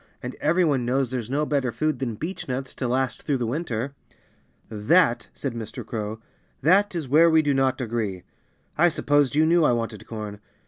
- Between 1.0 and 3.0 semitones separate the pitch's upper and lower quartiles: No, average, 4.6 semitones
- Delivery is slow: No, average, 190 wpm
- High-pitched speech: No, low, 130 Hz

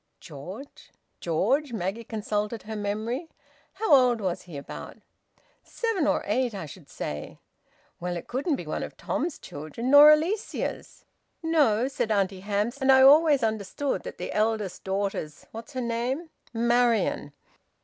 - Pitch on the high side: Yes, high, 225 Hz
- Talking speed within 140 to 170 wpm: Yes, average, 145 wpm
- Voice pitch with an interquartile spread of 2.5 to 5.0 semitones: No, wide, 5.5 semitones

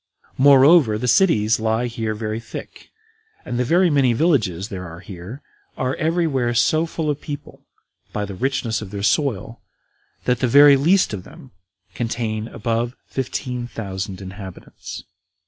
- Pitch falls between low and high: No, low, 120 Hz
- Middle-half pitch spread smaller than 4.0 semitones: No, average, 4.8 semitones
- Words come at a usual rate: Yes, average, 150 wpm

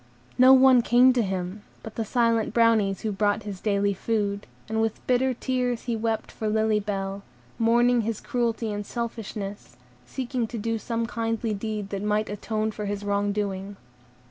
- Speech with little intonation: Yes, narrow, 2.2 semitones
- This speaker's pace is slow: No, average, 170 wpm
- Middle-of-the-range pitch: No, high, 220 Hz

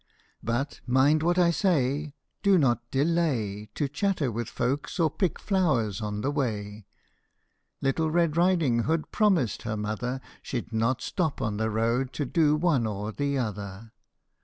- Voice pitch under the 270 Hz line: Yes, low, 135 Hz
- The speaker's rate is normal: Yes, average, 160 wpm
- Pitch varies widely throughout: Yes, wide, 6.3 semitones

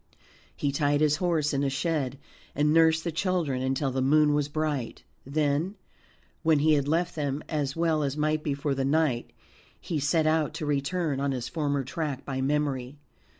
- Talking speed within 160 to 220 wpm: Yes, average, 185 wpm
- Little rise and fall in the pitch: Yes, narrow, 2.3 semitones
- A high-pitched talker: No, medium, 150 Hz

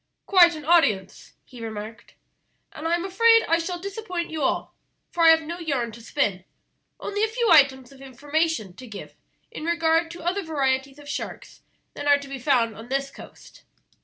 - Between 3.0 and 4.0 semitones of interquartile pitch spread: No, average, 4.6 semitones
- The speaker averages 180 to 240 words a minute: Yes, average, 185 wpm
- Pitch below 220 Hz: No, very high, 300 Hz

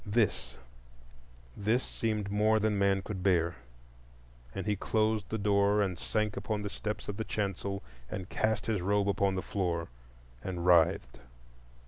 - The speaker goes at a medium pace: Yes, average, 150 wpm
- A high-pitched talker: No, low, 100 Hz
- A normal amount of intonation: No, narrow, 2.1 semitones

